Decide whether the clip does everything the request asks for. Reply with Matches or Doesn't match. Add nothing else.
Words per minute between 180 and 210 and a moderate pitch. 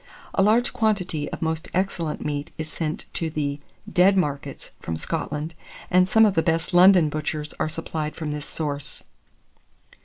Doesn't match